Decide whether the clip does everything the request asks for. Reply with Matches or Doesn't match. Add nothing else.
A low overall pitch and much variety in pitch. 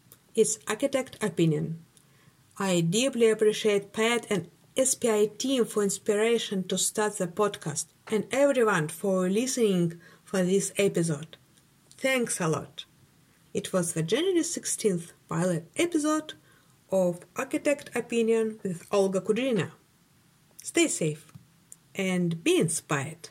Doesn't match